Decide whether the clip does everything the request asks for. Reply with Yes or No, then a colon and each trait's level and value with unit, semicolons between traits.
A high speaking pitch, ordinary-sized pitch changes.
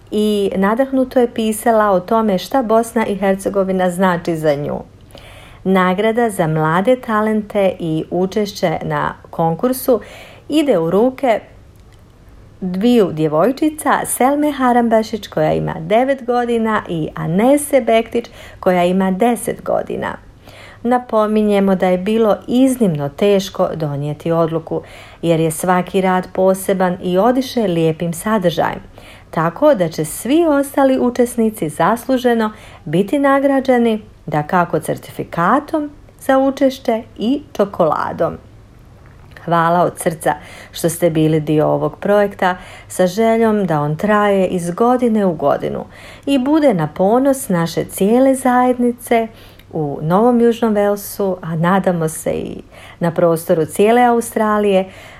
No: high, 200 Hz; wide, 6.2 semitones